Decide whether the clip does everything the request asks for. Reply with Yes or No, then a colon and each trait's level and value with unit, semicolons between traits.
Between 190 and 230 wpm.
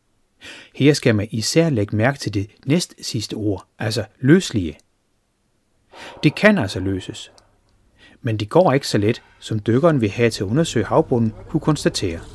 No: average, 160 wpm